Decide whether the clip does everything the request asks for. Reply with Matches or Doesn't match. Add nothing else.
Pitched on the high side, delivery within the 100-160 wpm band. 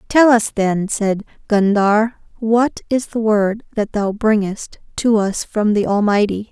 Matches